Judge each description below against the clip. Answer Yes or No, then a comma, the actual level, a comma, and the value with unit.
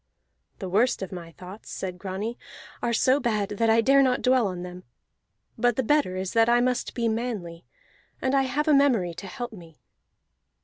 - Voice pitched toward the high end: Yes, high, 225 Hz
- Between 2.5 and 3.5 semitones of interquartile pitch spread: No, average, 5.3 semitones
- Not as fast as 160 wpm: No, average, 190 wpm